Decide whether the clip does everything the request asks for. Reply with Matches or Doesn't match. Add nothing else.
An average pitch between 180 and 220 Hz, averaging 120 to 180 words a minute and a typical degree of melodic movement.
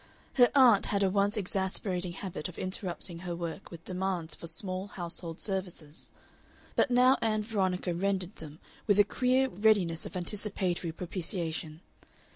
Matches